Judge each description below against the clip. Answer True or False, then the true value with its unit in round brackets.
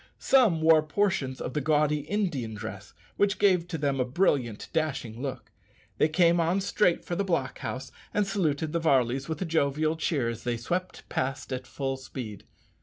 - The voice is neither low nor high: True (150 Hz)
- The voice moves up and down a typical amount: True (4.9 semitones)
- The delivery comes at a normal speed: True (180 wpm)